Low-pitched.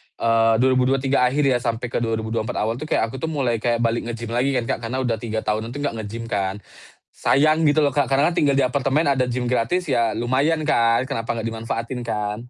Yes: low, 120 Hz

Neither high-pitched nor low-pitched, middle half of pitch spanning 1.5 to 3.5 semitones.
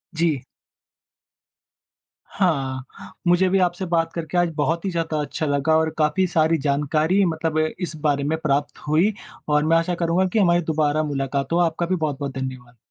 Yes: medium, 160 Hz; average, 2.9 semitones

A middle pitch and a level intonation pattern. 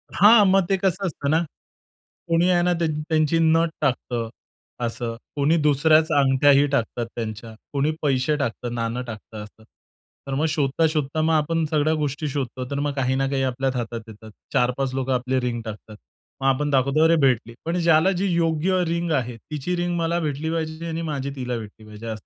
No: medium, 145 Hz; average, 4.5 semitones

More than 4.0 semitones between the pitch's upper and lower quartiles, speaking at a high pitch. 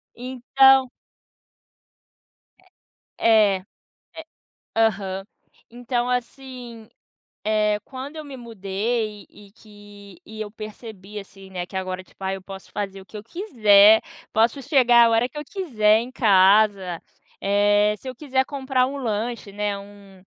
No: average, 3.7 semitones; high, 215 Hz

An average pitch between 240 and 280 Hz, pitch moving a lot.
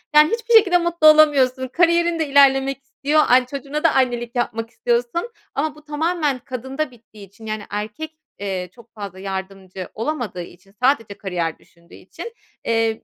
Yes: very high, 255 Hz; wide, 6.3 semitones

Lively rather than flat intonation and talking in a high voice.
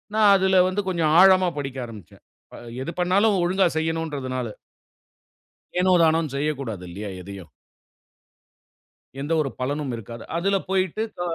No: wide, 6.4 semitones; medium, 160 Hz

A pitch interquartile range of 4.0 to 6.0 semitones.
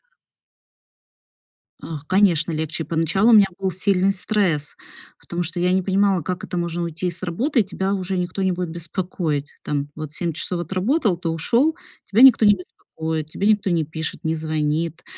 No: average, 3.3 semitones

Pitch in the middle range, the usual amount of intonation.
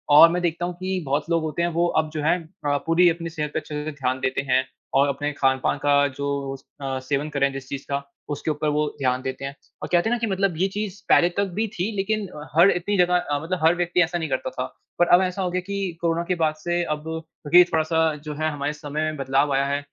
Yes: medium, 155 Hz; average, 3.7 semitones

